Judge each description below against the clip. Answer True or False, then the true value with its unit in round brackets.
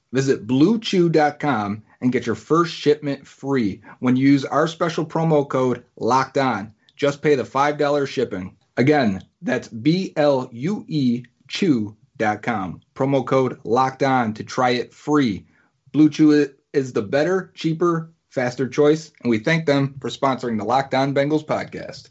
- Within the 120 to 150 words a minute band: True (140 wpm)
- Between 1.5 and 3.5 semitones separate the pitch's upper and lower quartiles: True (3.2 semitones)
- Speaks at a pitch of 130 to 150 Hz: True (135 Hz)